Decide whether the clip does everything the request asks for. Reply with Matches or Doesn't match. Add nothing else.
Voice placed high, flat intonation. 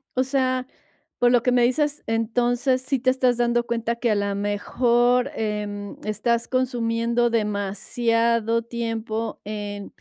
Matches